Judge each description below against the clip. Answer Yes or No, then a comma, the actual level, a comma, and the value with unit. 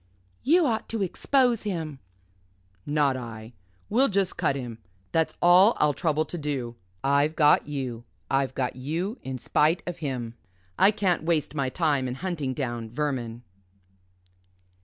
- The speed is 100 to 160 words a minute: Yes, average, 145 wpm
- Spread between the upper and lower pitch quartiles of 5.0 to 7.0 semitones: Yes, wide, 5.4 semitones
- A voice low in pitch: No, medium, 150 Hz